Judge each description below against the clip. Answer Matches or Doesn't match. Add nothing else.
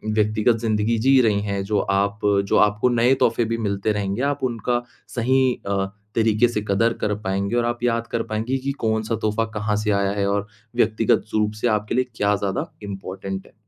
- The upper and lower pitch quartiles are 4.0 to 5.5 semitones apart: Doesn't match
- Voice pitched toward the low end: Matches